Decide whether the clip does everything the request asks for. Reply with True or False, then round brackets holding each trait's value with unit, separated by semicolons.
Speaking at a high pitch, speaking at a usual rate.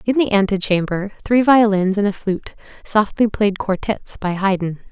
True (205 Hz; 160 wpm)